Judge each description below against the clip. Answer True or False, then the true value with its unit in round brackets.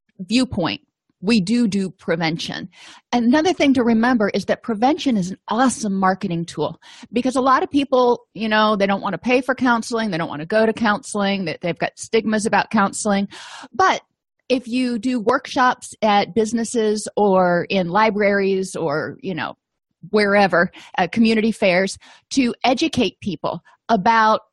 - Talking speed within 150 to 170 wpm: True (160 wpm)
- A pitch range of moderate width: True (3.7 semitones)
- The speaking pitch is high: True (220 Hz)